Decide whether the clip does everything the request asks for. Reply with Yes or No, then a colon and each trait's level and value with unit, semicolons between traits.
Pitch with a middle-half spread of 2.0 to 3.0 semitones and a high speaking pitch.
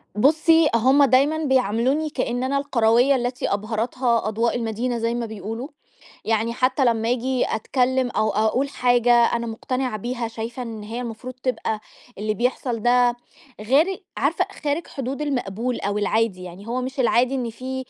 Yes: average, 2.7 semitones; high, 245 Hz